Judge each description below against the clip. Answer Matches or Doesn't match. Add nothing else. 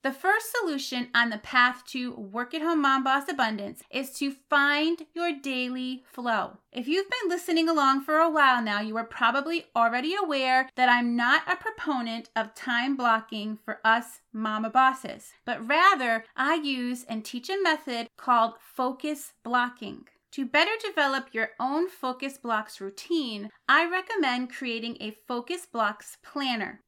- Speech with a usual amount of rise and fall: Matches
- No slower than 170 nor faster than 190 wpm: Doesn't match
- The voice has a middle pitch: Doesn't match